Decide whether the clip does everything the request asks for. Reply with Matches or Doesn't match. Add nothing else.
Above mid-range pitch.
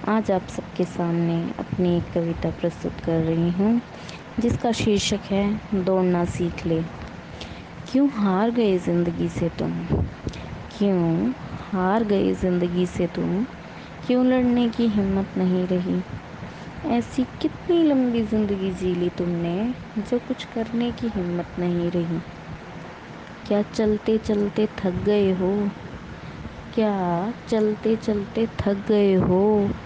Matches